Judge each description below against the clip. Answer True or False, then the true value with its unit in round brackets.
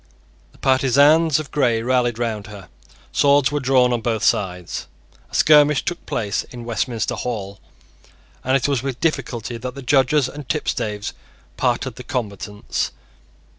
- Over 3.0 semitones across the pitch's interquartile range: True (3.7 semitones)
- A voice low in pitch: True (125 Hz)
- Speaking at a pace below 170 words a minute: True (145 wpm)